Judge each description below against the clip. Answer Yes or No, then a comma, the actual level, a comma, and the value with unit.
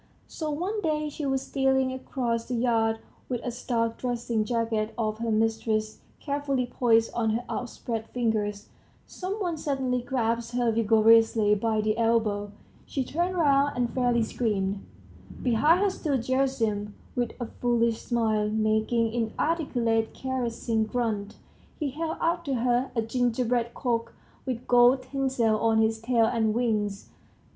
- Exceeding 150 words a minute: No, average, 145 wpm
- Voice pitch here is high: Yes, high, 235 Hz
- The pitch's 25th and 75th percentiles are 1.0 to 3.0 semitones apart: Yes, average, 2.7 semitones